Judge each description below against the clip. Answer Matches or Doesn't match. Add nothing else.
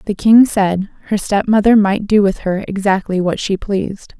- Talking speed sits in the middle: Matches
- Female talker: Matches